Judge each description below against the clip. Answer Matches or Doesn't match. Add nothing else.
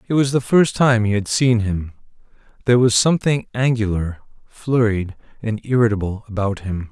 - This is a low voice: Matches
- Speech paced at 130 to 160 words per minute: Matches